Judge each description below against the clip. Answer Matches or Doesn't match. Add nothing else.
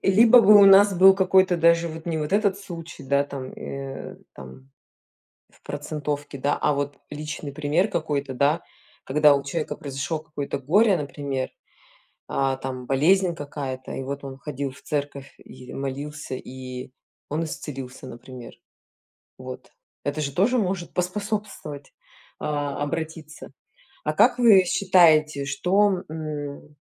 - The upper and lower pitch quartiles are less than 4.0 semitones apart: Doesn't match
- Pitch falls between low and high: Matches